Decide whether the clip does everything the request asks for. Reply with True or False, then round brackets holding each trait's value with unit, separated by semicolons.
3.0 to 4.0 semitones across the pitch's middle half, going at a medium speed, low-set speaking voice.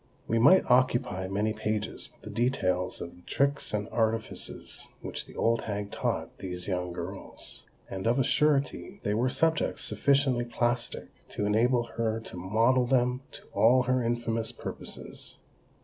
True (3.5 semitones; 155 wpm; 115 Hz)